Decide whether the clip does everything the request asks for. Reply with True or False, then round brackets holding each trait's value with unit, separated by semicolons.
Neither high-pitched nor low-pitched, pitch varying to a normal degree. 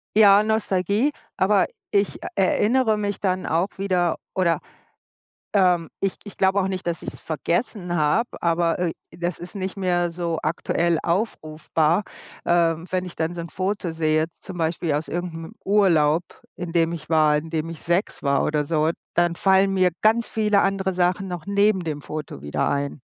True (175 Hz; 3.1 semitones)